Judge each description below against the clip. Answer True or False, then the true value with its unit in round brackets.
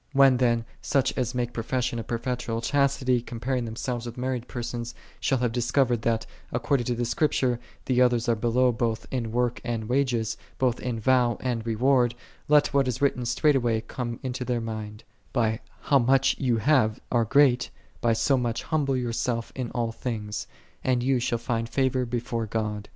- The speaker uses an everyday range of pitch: False (1.9 semitones)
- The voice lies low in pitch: True (120 Hz)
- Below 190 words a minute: True (180 wpm)